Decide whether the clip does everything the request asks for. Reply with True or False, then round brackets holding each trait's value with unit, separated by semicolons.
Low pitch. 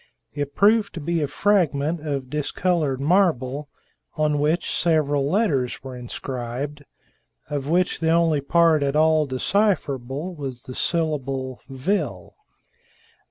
False (150 Hz)